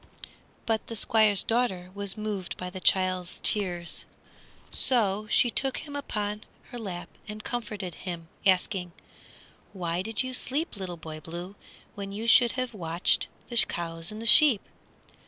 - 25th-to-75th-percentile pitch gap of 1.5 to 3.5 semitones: No, average, 4.1 semitones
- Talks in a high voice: Yes, high, 200 Hz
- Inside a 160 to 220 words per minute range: No, average, 150 wpm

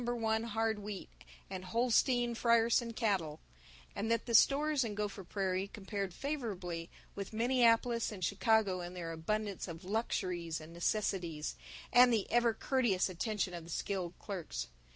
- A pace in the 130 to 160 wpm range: Yes, average, 145 wpm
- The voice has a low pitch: No, high, 210 Hz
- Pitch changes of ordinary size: Yes, average, 4.2 semitones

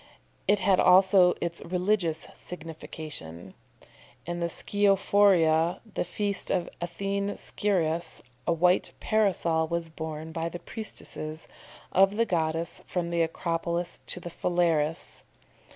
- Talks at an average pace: No, slow, 120 wpm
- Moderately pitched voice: Yes, medium, 175 Hz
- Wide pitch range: No, average, 3.0 semitones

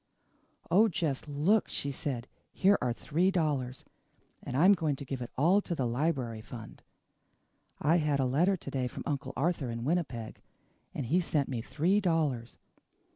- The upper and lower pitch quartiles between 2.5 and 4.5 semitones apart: No, average, 5.2 semitones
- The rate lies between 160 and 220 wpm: Yes, average, 170 wpm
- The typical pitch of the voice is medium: Yes, medium, 145 Hz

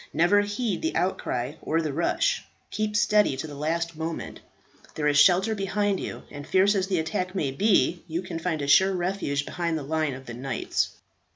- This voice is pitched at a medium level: Yes, medium, 170 Hz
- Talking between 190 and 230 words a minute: Yes, average, 195 wpm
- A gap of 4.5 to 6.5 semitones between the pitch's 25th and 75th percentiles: Yes, average, 4.8 semitones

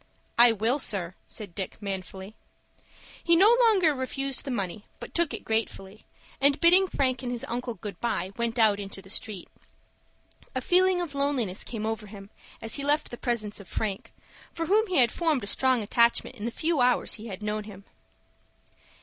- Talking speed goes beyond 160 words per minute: Yes, average, 185 wpm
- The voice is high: Yes, high, 235 Hz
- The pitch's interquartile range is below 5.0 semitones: No, average, 5.3 semitones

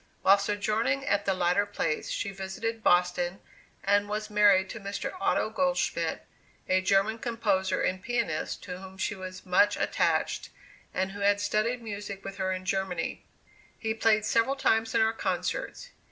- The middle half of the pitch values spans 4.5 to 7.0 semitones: No, average, 2.7 semitones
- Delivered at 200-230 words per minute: No, average, 160 wpm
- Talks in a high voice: Yes, high, 205 Hz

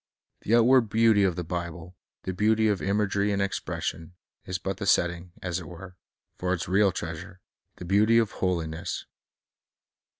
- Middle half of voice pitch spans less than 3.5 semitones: Yes, average, 3.0 semitones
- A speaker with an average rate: Yes, average, 170 wpm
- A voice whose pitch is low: Yes, very low, 95 Hz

